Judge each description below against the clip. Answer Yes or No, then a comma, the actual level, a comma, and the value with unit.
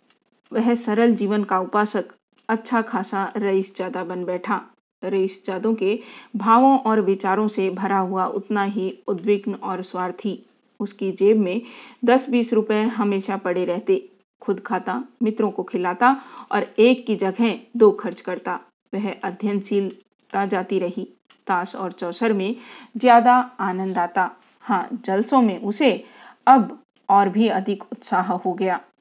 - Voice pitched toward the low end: No, high, 205 Hz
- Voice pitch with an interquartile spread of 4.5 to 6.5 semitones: No, average, 3.3 semitones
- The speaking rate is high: No, average, 140 wpm